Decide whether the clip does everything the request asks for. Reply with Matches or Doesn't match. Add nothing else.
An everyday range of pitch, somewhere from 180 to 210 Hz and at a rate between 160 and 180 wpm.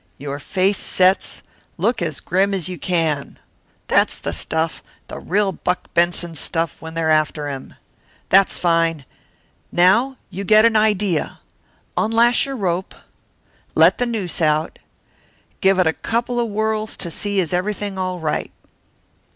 Doesn't match